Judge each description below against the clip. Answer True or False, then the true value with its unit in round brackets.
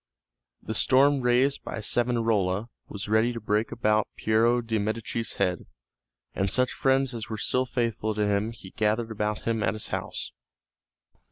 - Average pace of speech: True (160 wpm)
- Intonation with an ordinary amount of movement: False (2.3 semitones)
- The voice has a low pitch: True (110 Hz)